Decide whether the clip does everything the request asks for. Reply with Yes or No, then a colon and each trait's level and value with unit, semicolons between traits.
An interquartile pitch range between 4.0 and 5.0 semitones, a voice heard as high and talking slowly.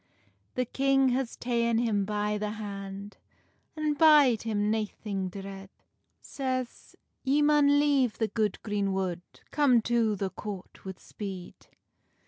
Yes: average, 4.7 semitones; high, 220 Hz; slow, 125 wpm